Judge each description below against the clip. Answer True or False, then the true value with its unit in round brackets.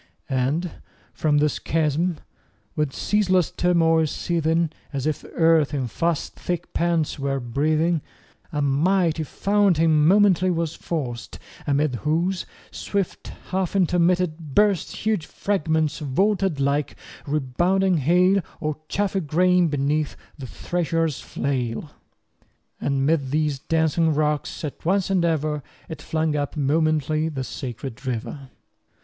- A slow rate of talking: True (125 wpm)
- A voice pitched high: False (155 Hz)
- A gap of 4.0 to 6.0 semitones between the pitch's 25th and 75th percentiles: False (3.4 semitones)